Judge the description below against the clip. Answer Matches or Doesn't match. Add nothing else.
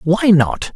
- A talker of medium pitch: Matches